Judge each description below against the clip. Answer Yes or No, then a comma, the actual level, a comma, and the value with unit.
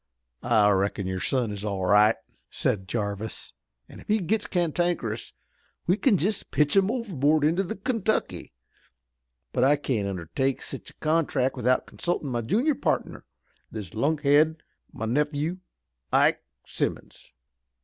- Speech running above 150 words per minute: No, average, 140 wpm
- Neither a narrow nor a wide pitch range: No, wide, 8.2 semitones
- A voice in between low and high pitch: Yes, medium, 145 Hz